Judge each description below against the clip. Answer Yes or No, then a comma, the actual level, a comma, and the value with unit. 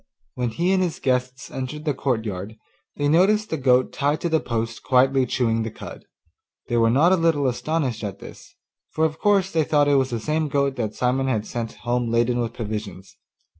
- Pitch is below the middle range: Yes, low, 130 Hz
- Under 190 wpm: No, fast, 205 wpm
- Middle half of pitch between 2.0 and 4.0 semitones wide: No, average, 4.7 semitones